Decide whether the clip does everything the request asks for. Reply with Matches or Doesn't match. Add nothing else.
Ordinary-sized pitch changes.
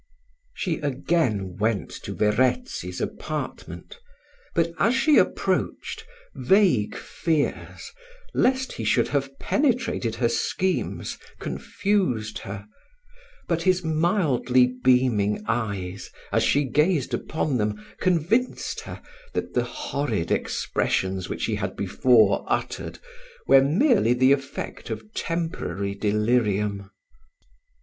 Doesn't match